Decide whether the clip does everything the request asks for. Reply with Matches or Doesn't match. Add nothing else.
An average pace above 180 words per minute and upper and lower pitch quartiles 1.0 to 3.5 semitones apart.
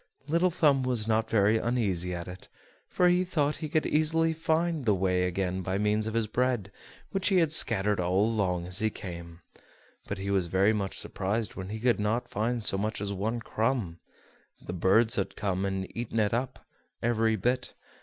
Doesn't match